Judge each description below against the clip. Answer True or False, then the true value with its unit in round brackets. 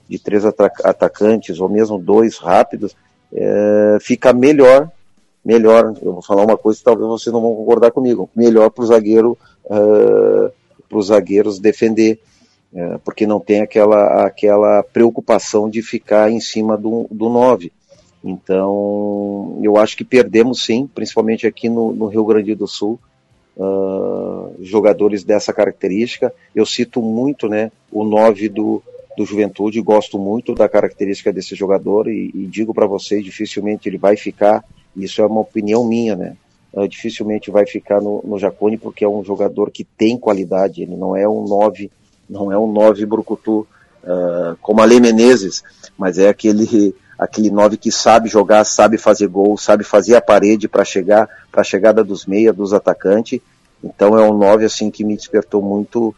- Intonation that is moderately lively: False (1.7 semitones)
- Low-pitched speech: True (105 Hz)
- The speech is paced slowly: False (165 wpm)